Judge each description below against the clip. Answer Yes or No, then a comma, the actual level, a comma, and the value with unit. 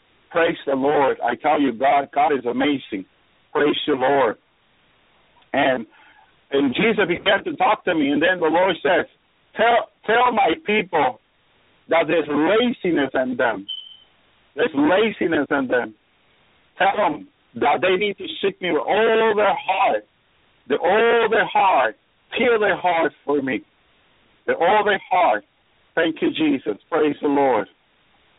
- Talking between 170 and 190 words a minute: No, average, 150 wpm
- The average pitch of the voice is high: Yes, high, 210 Hz